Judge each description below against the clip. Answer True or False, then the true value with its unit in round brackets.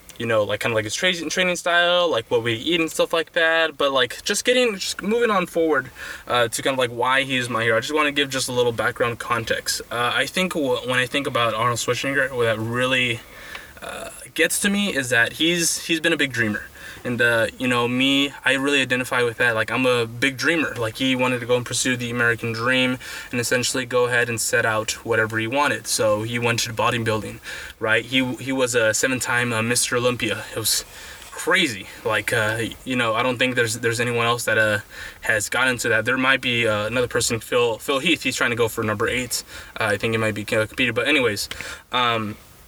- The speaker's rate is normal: False (230 wpm)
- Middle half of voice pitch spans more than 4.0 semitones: True (4.6 semitones)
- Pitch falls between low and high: False (125 Hz)